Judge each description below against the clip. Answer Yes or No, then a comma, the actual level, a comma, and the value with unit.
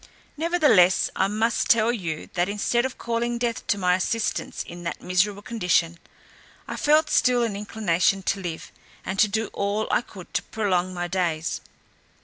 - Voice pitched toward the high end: Yes, high, 200 Hz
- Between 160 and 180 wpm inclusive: Yes, average, 165 wpm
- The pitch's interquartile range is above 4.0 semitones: Yes, average, 4.4 semitones